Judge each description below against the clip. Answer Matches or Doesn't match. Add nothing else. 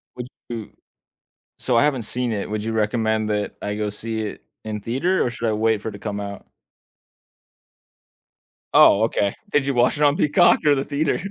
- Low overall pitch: Matches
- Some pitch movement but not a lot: Matches